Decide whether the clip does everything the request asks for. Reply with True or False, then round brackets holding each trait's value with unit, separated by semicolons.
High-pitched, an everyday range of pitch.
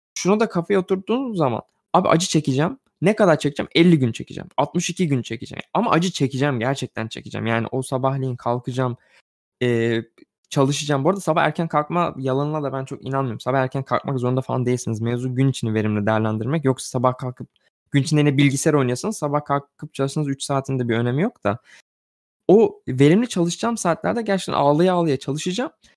False (140 Hz; 5.0 semitones)